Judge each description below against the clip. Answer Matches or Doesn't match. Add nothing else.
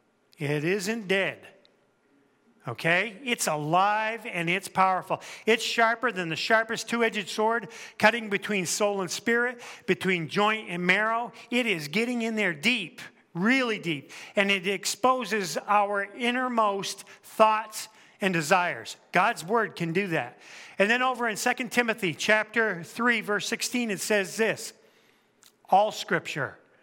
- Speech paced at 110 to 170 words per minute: Matches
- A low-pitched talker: Doesn't match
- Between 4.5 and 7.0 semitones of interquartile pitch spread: Doesn't match